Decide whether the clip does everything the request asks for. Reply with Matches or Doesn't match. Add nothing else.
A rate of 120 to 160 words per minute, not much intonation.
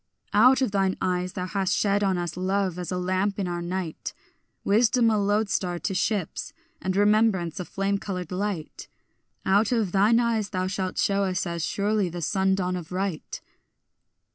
Doesn't match